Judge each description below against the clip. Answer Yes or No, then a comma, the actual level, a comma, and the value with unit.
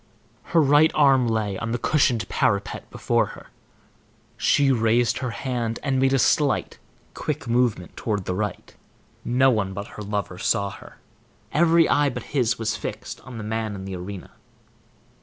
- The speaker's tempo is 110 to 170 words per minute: Yes, average, 165 wpm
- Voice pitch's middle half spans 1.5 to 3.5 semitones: No, average, 4.4 semitones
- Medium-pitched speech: No, low, 115 Hz